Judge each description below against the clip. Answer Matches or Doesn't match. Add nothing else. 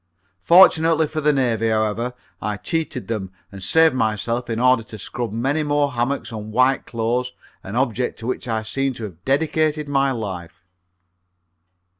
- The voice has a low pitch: Matches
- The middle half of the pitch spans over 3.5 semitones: Matches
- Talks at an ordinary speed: Matches